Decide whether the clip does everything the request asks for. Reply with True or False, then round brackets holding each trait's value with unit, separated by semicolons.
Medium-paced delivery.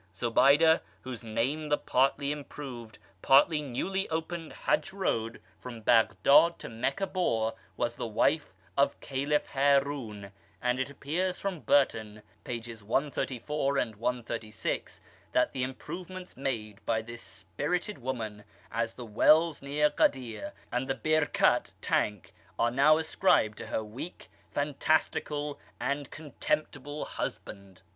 False (120 wpm)